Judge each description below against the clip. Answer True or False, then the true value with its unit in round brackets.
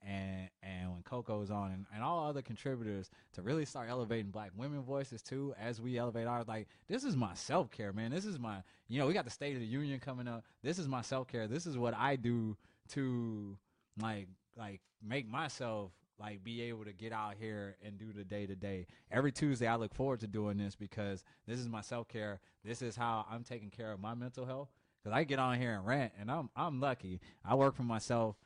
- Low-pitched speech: True (115 Hz)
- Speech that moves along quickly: True (230 wpm)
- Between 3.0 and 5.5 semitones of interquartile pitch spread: True (3.8 semitones)